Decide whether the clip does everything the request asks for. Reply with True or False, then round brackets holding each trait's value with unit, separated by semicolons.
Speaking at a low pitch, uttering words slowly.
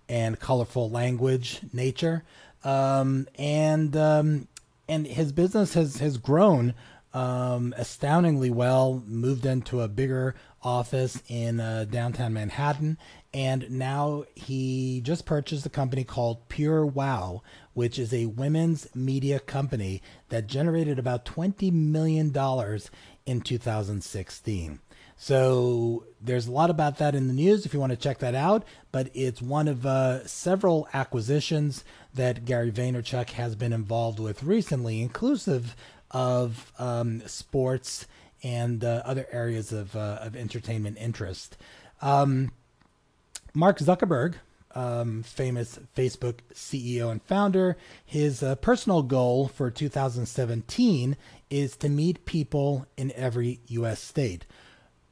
True (130 Hz; 130 wpm)